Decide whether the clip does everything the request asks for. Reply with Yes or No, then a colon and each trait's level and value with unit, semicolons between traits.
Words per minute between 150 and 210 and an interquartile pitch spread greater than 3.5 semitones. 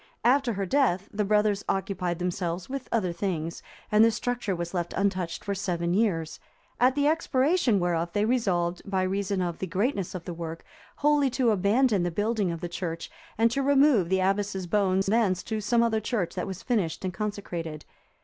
Yes: average, 190 wpm; average, 4.6 semitones